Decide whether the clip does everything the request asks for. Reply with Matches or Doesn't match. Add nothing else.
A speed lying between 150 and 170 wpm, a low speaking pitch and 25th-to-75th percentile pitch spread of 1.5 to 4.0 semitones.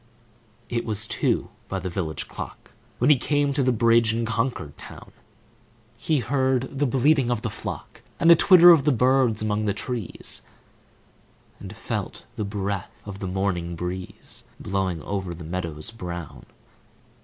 Doesn't match